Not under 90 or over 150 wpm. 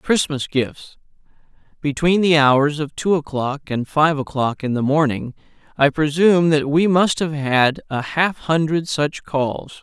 No: average, 160 wpm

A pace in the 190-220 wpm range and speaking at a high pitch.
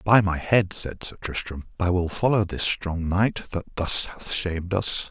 No: average, 200 wpm; very low, 90 Hz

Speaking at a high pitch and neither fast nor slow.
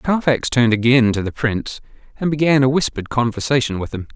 No: low, 125 Hz; average, 190 wpm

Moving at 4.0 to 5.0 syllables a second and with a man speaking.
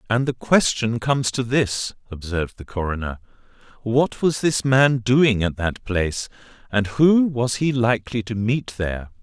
Yes: 4.5 syllables/s; male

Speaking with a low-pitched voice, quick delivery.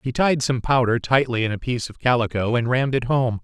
Yes: low, 120 Hz; fast, 245 wpm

